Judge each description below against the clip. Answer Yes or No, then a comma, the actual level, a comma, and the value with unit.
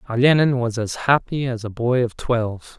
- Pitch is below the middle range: Yes, low, 120 Hz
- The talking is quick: No, average, 195 wpm